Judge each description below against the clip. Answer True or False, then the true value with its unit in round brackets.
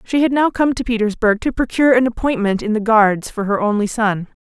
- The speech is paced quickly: True (230 wpm)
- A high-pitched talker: True (225 Hz)